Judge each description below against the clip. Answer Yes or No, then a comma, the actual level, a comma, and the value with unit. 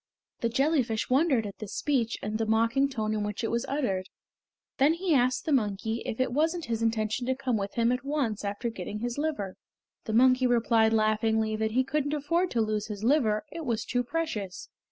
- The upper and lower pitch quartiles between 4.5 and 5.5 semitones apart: No, average, 3.9 semitones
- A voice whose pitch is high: Yes, high, 235 Hz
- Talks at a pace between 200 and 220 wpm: Yes, fast, 205 wpm